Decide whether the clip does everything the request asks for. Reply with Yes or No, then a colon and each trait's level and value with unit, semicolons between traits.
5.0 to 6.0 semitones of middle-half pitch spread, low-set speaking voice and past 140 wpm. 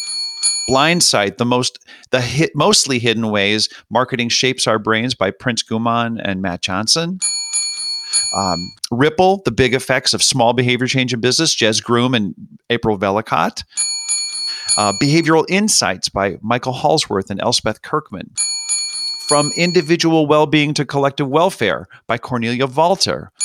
No: average, 5.3 semitones; low, 125 Hz; slow, 135 wpm